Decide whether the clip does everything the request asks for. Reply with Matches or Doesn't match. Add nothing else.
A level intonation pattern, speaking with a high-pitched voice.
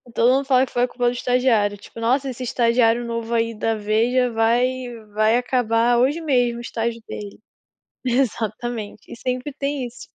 Matches